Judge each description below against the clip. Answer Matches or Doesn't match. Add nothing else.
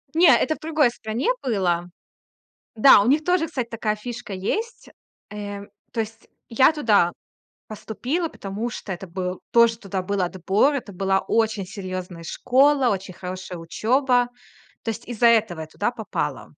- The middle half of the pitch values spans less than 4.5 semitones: Doesn't match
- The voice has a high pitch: Matches